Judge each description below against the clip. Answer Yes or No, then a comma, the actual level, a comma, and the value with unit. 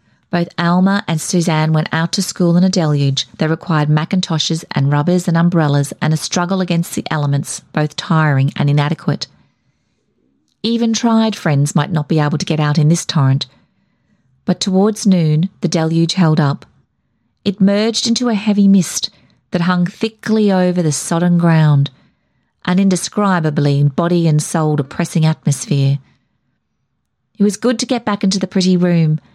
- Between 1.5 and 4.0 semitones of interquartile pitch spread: Yes, average, 3.7 semitones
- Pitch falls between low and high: Yes, medium, 170 Hz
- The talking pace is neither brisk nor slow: Yes, average, 160 wpm